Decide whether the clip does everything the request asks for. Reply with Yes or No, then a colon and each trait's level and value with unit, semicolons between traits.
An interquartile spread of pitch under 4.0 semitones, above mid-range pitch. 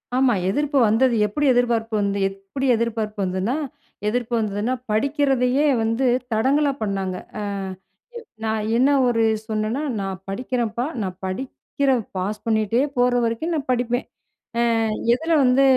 Yes: average, 3.6 semitones; high, 235 Hz